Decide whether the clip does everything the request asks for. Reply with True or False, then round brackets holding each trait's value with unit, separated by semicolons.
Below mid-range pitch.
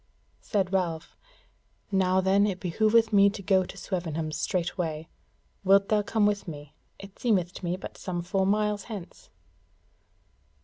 False (190 Hz)